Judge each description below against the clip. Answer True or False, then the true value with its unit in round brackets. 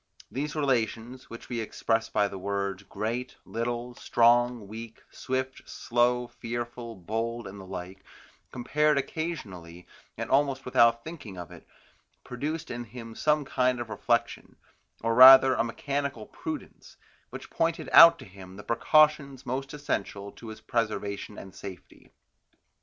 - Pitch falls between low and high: False (120 Hz)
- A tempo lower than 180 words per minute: True (140 wpm)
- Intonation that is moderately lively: True (3.7 semitones)